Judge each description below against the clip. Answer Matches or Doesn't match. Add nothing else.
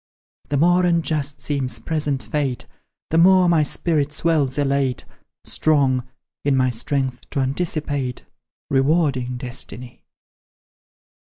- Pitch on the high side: Doesn't match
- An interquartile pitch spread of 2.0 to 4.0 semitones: Matches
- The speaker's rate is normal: Doesn't match